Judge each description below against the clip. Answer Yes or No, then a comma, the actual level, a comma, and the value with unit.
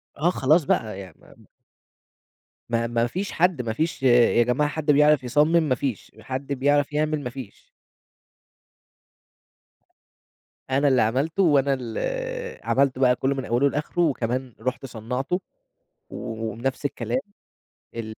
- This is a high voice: No, low, 135 Hz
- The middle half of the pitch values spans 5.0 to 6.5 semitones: No, average, 3.5 semitones